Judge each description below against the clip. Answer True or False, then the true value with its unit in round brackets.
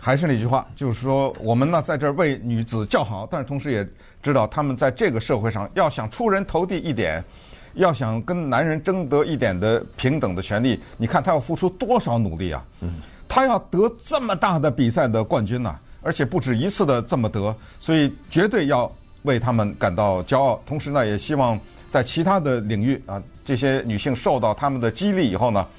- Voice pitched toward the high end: False (130 Hz)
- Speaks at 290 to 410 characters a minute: True (305 characters per minute)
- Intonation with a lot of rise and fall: True (6.4 semitones)